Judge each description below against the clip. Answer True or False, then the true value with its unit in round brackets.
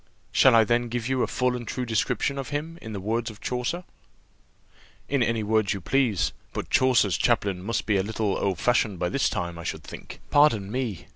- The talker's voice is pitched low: True (115 Hz)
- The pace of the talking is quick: True (210 wpm)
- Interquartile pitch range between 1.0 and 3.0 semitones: False (3.8 semitones)